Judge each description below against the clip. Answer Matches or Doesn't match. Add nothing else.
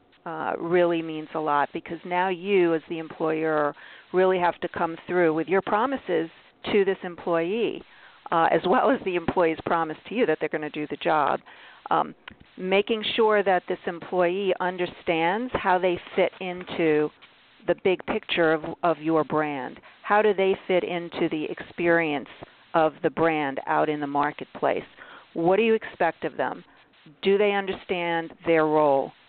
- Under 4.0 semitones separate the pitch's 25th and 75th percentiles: Matches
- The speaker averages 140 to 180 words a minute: Matches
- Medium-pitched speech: Matches